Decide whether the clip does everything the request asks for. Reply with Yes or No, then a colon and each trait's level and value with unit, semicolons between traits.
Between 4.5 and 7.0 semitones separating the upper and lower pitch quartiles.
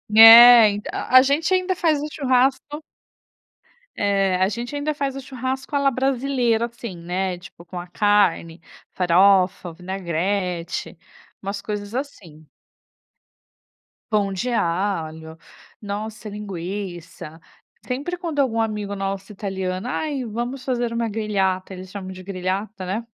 Yes: average, 5.2 semitones